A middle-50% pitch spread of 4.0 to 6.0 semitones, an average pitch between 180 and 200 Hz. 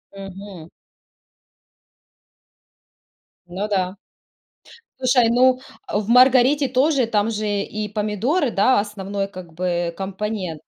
No: average, 4.3 semitones; high, 210 Hz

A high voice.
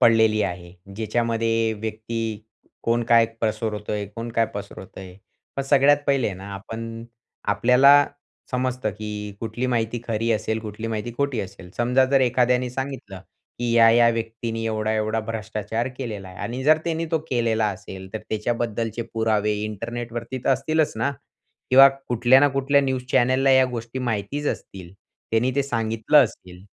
No: low, 115 Hz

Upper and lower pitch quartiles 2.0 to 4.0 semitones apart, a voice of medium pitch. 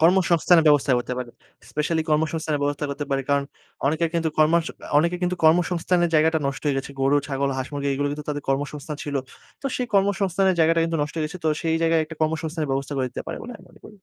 Yes: average, 2.7 semitones; medium, 155 Hz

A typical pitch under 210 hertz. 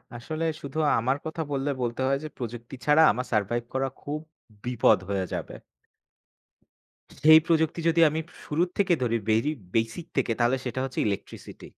Yes: low, 135 Hz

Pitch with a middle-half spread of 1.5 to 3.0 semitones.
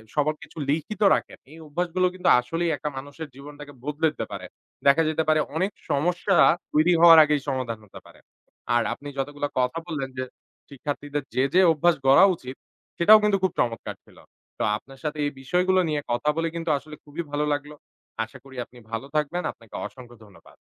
No: average, 3.5 semitones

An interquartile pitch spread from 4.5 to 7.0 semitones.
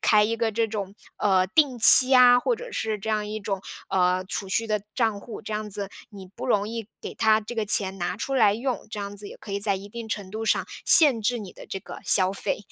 No: narrow, 2.5 semitones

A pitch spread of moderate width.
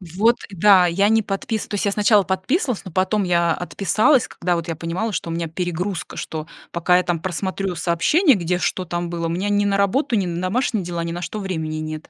Yes: average, 3.2 semitones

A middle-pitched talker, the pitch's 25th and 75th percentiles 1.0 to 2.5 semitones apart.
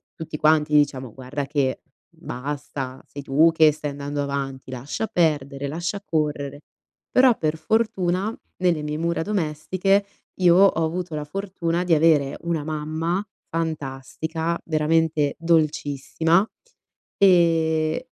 No: medium, 155 Hz; average, 2.9 semitones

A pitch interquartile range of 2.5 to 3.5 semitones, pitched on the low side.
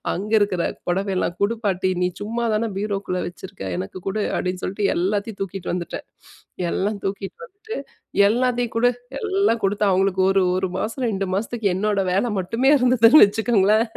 No: average, 3.2 semitones; high, 205 Hz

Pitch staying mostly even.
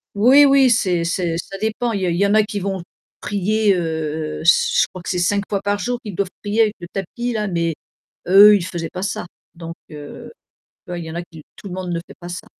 No: average, 3.4 semitones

